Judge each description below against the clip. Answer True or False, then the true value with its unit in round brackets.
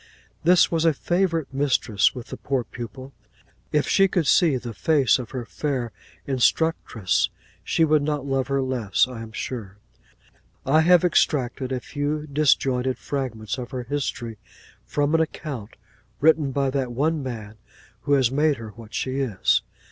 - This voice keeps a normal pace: True (160 wpm)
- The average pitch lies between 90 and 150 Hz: True (135 Hz)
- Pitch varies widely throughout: False (3.8 semitones)